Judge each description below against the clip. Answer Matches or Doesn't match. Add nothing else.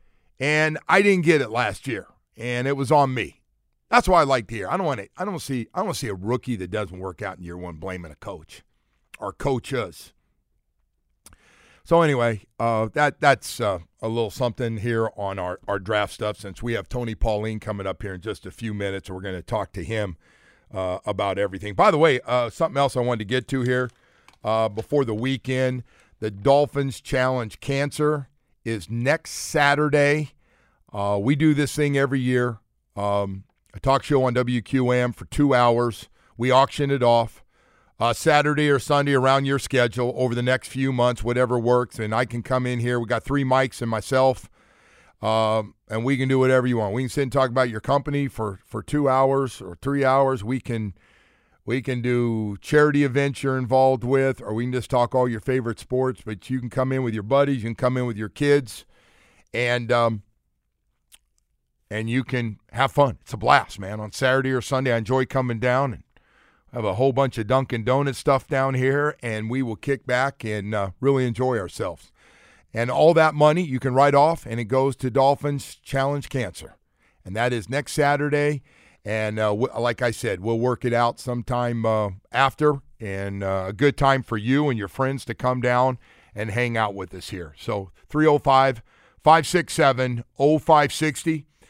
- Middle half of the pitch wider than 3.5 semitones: Matches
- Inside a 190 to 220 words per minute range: Matches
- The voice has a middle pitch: Doesn't match